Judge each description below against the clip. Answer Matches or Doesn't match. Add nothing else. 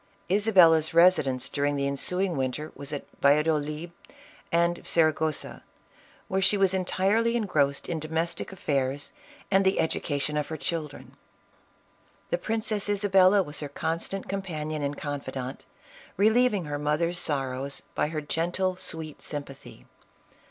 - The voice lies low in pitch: Doesn't match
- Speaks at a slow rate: Matches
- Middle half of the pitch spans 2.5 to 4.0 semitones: Doesn't match